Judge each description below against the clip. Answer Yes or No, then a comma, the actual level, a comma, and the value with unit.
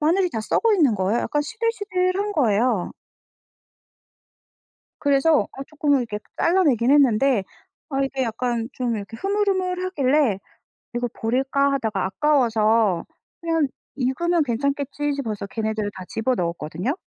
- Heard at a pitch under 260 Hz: No, very high, 270 Hz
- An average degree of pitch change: No, wide, 5.9 semitones